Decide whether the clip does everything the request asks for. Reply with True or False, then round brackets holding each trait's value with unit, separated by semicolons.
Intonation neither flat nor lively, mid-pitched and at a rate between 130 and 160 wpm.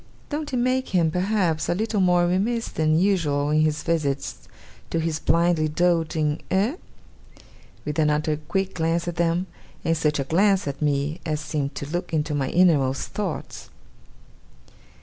True (3.4 semitones; 165 Hz; 155 wpm)